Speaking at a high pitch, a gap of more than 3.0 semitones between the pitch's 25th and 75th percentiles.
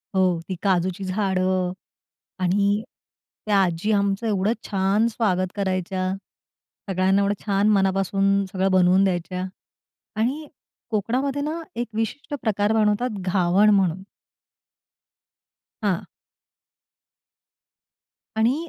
No: high, 195 Hz; narrow, 2.4 semitones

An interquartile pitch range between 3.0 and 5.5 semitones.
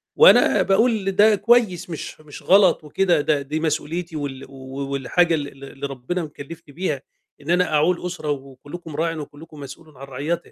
Yes: average, 4.0 semitones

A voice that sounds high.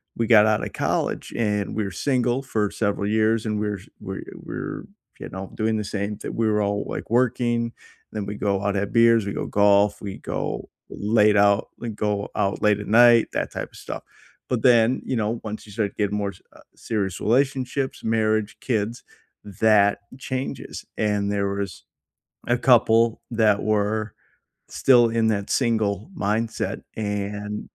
No: low, 105 Hz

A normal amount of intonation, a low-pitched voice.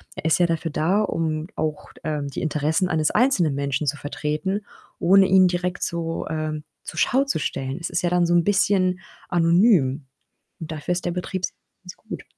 No: average, 3.2 semitones; medium, 165 Hz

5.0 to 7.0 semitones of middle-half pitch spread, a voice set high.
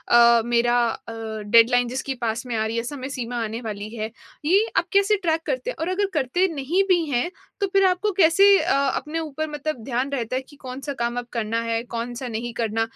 Yes: wide, 5.6 semitones; very high, 250 Hz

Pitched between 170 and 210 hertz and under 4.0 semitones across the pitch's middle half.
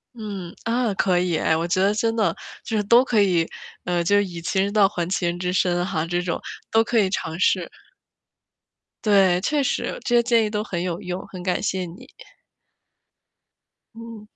Yes: high, 190 Hz; average, 3.5 semitones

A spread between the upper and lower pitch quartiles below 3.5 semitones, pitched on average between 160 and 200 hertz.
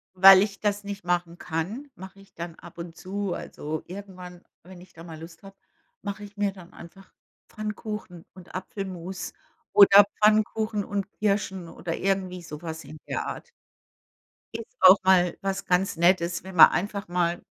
Yes: narrow, 2.6 semitones; medium, 185 Hz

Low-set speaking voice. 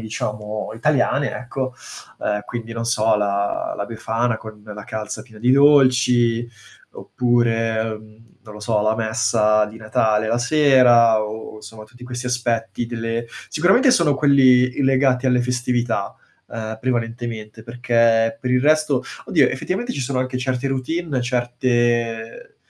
Yes: low, 120 Hz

